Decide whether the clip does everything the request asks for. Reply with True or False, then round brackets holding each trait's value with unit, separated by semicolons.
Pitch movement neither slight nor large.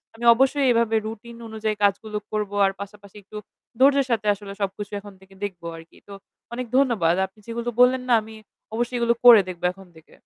True (3.0 semitones)